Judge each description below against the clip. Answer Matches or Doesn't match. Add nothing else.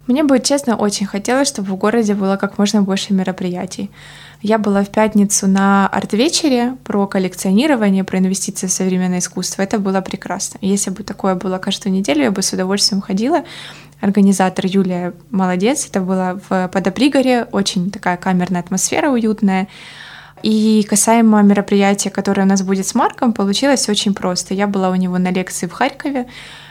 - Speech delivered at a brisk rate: Matches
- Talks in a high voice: Matches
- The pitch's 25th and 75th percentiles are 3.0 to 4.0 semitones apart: Doesn't match